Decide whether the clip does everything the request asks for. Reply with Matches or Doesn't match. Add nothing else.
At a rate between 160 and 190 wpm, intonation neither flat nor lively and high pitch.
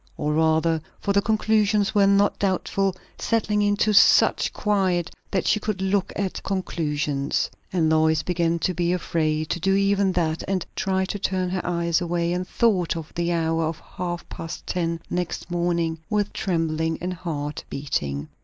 Doesn't match